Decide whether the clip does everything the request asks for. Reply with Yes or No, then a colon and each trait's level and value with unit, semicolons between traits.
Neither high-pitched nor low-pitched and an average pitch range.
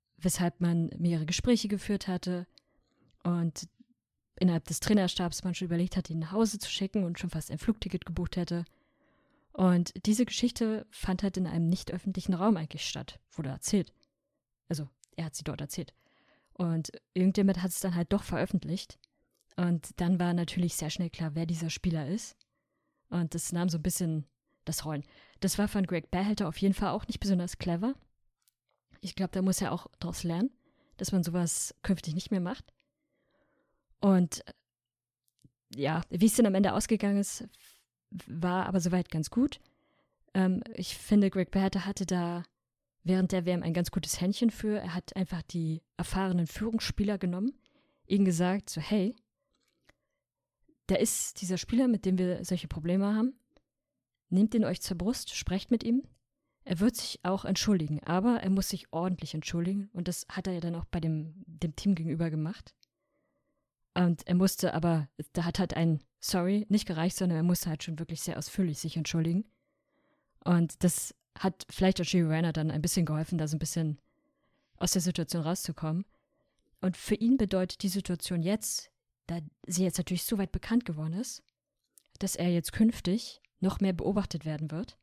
Yes: medium, 180 Hz; average, 3.1 semitones